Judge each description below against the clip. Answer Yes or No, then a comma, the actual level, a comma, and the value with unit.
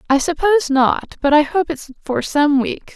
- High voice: Yes, very high, 300 Hz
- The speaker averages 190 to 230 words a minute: Yes, fast, 205 wpm